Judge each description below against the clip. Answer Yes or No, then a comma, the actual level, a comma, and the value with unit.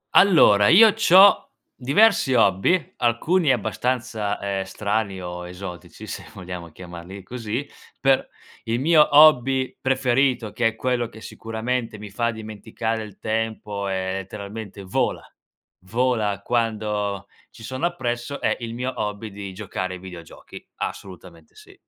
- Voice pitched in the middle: No, low, 110 Hz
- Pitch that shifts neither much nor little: Yes, average, 4.2 semitones